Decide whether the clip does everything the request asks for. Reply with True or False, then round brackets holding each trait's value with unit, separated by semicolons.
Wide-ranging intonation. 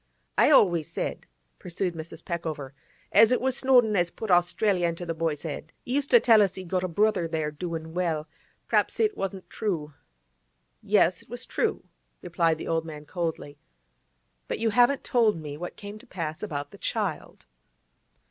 False (4.7 semitones)